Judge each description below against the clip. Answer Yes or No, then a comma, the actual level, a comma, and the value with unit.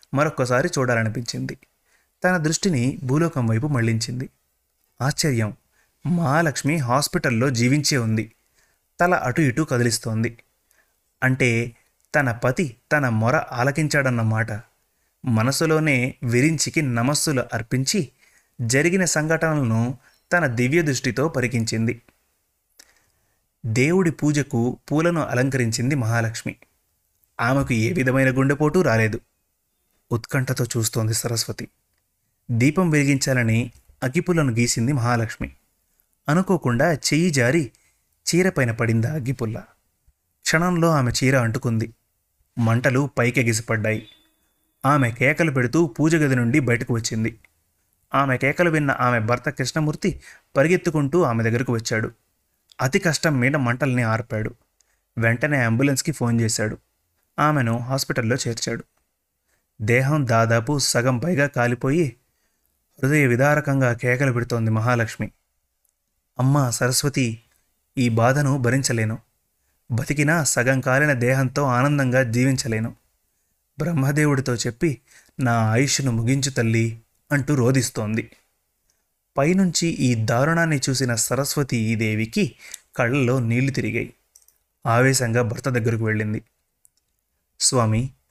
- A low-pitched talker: Yes, low, 125 Hz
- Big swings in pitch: No, average, 4.0 semitones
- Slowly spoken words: No, average, 95 wpm